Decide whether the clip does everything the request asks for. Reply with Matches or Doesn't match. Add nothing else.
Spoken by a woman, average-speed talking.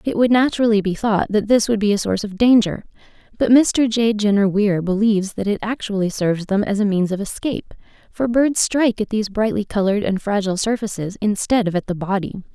Doesn't match